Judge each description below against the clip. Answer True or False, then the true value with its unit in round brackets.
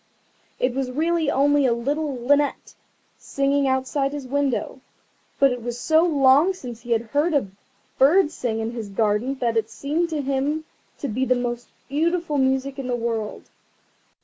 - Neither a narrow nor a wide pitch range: True (3.2 semitones)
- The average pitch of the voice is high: True (270 Hz)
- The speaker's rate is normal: True (170 wpm)